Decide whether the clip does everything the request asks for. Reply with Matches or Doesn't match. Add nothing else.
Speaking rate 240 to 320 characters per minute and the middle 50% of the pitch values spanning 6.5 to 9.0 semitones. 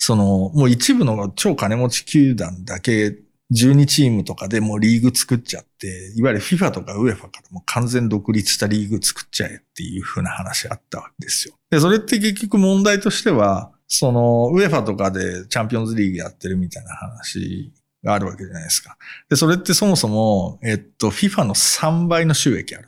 Doesn't match